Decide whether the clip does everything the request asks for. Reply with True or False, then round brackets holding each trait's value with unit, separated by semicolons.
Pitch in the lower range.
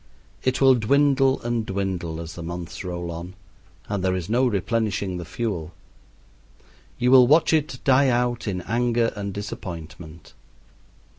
True (105 Hz)